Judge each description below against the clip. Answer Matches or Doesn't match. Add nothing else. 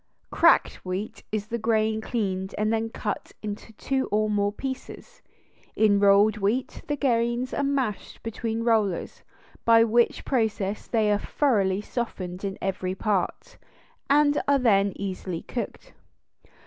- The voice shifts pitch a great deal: Doesn't match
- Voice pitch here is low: Doesn't match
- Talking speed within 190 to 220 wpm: Doesn't match